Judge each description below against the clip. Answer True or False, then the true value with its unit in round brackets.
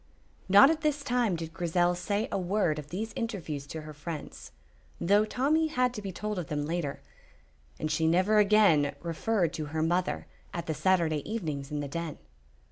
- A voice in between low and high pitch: True (175 Hz)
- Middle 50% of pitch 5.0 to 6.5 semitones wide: True (5.3 semitones)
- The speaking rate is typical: True (185 wpm)